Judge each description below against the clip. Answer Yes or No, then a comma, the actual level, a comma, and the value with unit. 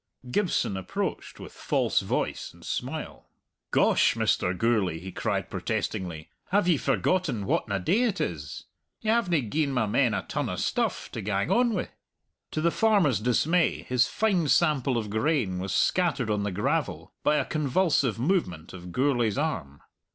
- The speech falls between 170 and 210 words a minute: No, average, 160 wpm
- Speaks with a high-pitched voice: No, low, 125 Hz